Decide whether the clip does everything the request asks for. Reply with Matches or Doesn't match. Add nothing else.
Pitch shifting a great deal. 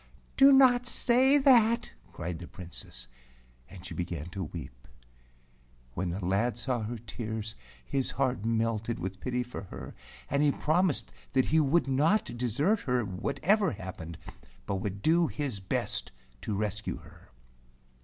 Matches